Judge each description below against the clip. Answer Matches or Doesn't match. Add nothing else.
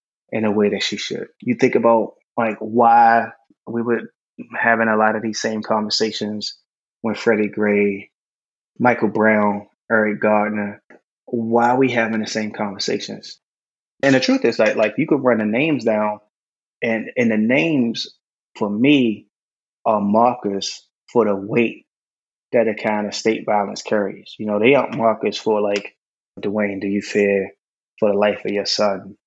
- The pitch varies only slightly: Matches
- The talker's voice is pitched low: Matches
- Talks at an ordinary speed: Matches